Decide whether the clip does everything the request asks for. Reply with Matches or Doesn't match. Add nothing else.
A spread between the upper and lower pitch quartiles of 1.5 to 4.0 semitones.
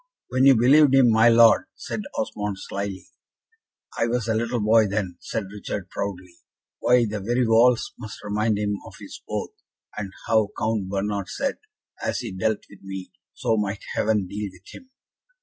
Matches